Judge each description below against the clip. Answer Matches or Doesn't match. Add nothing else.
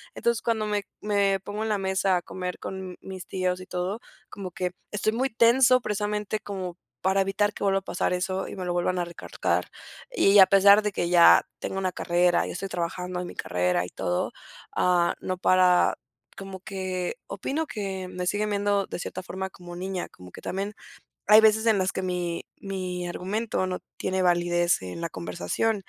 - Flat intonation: Matches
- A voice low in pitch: Doesn't match